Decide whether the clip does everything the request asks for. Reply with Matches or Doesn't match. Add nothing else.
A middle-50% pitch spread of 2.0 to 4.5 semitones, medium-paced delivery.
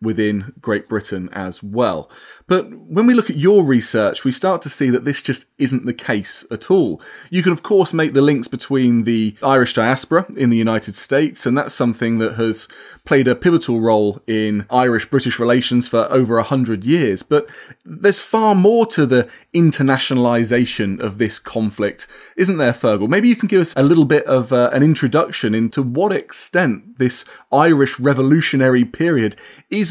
Doesn't match